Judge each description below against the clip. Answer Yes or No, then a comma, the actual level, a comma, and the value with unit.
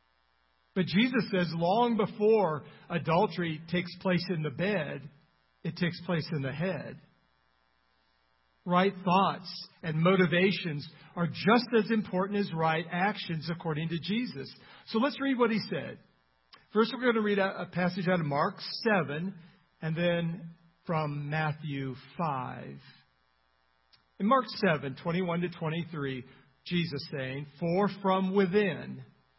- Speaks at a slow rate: Yes, slow, 130 wpm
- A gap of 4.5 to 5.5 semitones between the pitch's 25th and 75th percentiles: Yes, average, 4.8 semitones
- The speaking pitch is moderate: Yes, medium, 170 Hz